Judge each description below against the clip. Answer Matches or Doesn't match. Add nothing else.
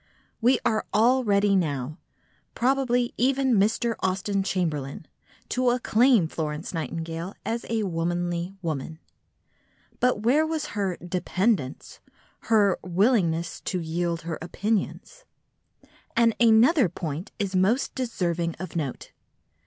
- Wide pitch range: Matches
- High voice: Matches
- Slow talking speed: Matches